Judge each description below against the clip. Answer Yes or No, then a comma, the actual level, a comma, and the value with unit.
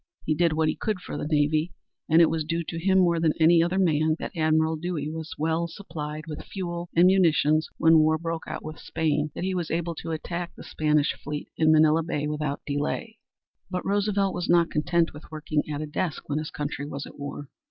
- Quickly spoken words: Yes, fast, 225 wpm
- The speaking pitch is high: No, medium, 160 Hz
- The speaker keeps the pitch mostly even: Yes, narrow, 2.1 semitones